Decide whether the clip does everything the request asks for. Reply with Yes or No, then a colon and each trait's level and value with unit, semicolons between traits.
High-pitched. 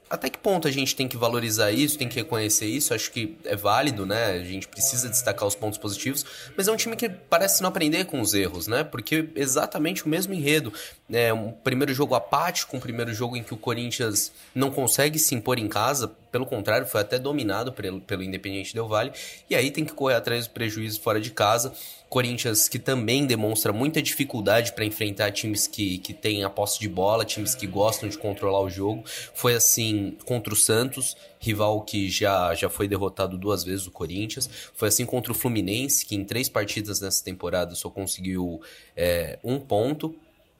No: low, 115 Hz